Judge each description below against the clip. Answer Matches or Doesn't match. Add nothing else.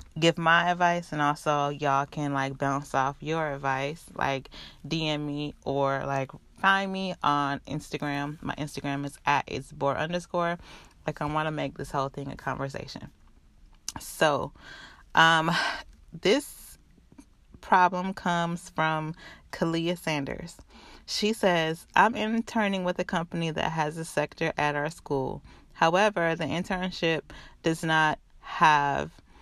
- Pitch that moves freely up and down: Doesn't match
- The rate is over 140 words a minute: Doesn't match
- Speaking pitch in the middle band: Matches